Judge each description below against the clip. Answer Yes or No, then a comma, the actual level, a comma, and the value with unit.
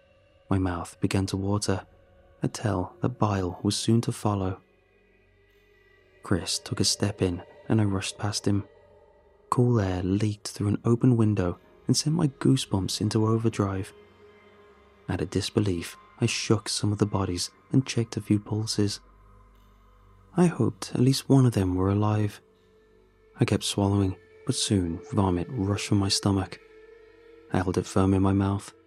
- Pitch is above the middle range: No, low, 105 Hz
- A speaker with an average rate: Yes, average, 160 wpm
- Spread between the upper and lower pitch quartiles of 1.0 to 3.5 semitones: Yes, average, 2.9 semitones